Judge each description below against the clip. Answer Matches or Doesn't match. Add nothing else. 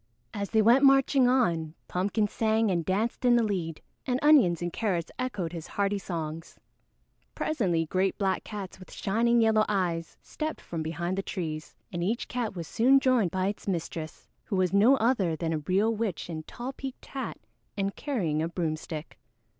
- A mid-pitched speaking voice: Doesn't match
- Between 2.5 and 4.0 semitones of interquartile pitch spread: Doesn't match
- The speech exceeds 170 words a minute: Matches